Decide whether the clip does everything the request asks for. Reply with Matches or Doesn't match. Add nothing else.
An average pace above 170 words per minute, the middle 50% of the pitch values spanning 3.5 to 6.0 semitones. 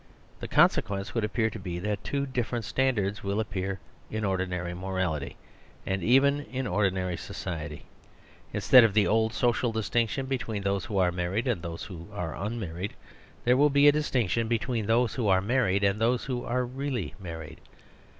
Matches